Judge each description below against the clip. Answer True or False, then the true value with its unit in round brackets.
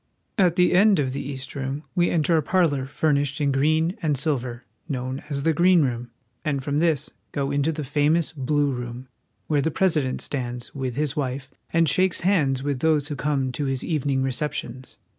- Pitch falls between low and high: True (145 Hz)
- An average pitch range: True (3.1 semitones)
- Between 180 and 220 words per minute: True (190 wpm)